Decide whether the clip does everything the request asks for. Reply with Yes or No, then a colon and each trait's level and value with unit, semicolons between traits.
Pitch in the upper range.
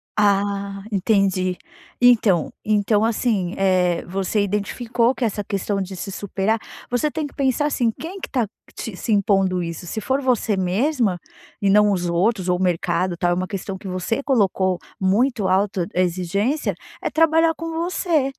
Yes: high, 200 Hz